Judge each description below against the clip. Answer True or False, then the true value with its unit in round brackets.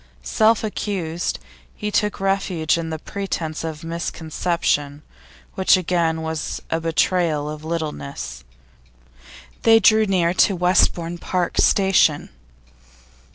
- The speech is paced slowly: True (110 wpm)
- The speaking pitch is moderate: True (170 Hz)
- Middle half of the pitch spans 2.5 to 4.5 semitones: True (3.3 semitones)